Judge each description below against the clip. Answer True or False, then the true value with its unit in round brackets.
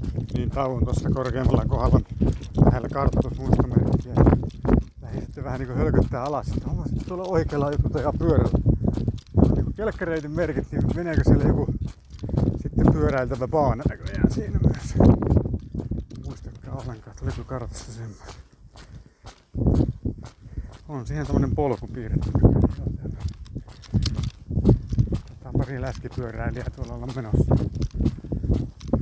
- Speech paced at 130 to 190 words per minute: False (110 wpm)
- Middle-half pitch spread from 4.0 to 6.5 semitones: False (3.1 semitones)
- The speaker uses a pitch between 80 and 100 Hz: False (125 Hz)